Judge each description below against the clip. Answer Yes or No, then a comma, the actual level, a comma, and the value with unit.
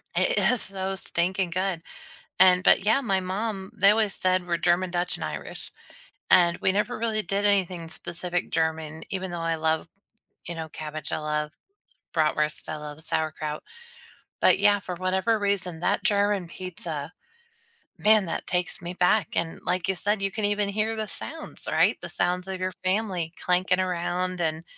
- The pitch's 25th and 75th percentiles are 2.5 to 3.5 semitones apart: Yes, average, 3.0 semitones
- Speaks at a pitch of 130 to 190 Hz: Yes, medium, 185 Hz